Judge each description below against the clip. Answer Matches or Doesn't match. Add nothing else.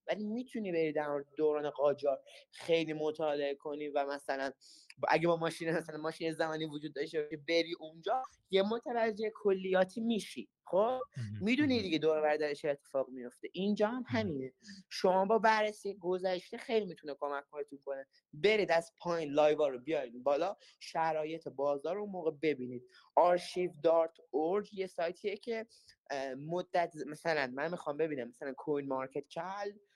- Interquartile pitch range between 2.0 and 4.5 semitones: Doesn't match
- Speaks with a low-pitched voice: Doesn't match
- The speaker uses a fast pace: Doesn't match